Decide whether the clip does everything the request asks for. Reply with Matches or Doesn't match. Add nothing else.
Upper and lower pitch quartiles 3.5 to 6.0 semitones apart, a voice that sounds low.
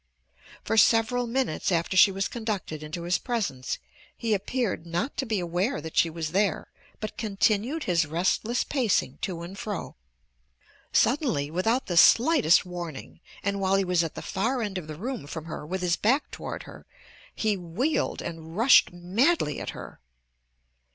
Doesn't match